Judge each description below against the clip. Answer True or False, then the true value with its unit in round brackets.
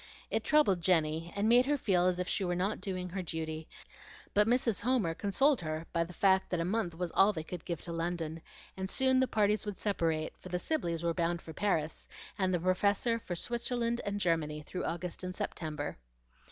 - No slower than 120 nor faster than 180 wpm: False (205 wpm)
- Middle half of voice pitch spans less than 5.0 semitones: True (3.8 semitones)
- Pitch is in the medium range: True (180 Hz)